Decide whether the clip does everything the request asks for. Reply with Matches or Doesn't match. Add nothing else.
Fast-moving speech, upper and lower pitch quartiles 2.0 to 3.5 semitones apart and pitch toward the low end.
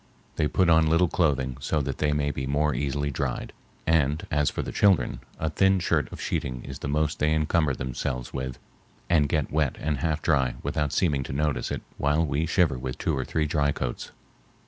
Matches